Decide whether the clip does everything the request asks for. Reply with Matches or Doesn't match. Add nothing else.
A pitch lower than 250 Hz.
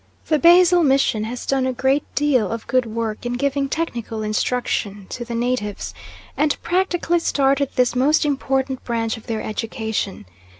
Doesn't match